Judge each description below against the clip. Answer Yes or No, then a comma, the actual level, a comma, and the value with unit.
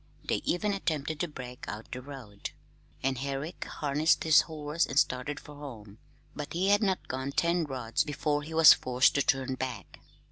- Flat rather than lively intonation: No, average, 3.5 semitones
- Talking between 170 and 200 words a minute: Yes, average, 180 wpm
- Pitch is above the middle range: No, medium, 145 Hz